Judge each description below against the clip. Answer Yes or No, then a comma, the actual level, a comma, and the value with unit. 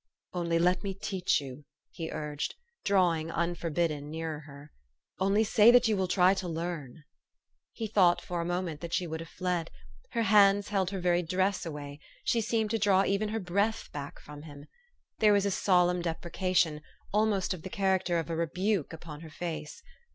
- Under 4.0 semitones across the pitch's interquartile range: Yes, average, 3.5 semitones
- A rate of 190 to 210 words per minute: Yes, average, 195 wpm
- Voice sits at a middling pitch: Yes, medium, 175 Hz